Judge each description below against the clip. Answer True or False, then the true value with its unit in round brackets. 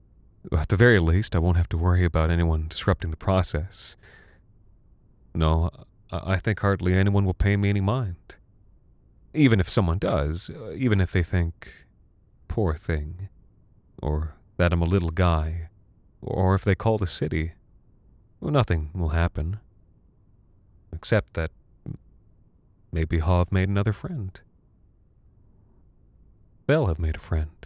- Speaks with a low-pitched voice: True (95 Hz)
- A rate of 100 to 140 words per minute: True (135 wpm)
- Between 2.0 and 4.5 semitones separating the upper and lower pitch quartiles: True (3.4 semitones)